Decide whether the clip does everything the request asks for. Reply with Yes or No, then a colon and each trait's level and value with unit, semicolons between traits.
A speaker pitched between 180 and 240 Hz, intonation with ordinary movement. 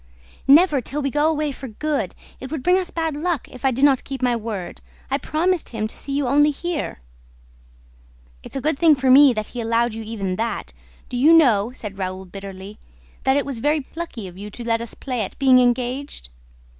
No: very high, 260 Hz; average, 4.7 semitones